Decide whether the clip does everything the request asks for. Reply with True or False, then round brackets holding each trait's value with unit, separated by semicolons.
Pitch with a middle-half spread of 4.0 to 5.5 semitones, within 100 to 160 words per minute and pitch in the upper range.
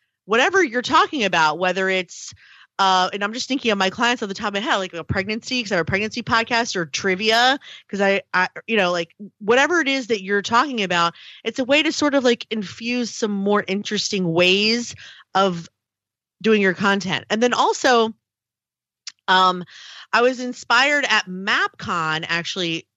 False (4.5 semitones; 185 wpm; 210 Hz)